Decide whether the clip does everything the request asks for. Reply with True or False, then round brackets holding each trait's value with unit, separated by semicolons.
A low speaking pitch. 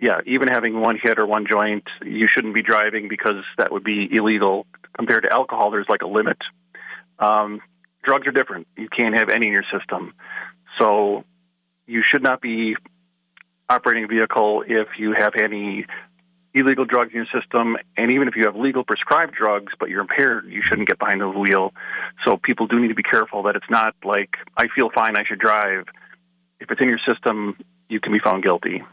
True (110 Hz)